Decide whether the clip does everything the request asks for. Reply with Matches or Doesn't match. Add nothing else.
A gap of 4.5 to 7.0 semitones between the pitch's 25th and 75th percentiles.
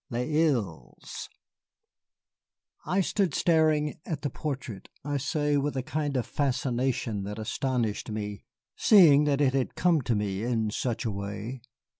Matches